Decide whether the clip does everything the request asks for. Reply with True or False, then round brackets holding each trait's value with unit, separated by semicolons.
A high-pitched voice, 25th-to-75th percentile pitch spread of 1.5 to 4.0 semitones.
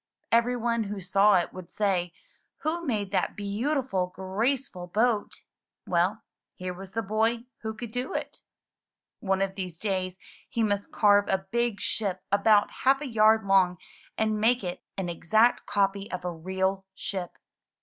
True (205 Hz; 3.1 semitones)